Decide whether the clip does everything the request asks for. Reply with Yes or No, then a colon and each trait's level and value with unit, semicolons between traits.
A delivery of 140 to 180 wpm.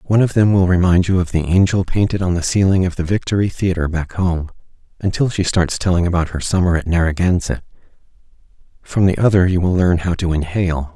No: fast, 205 wpm